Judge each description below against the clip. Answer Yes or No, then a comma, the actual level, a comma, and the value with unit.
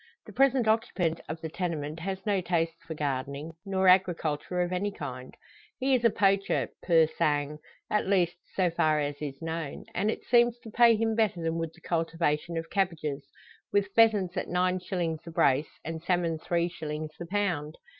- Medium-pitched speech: Yes, medium, 170 Hz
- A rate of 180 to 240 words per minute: Yes, average, 185 wpm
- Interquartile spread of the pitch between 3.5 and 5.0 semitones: Yes, average, 3.8 semitones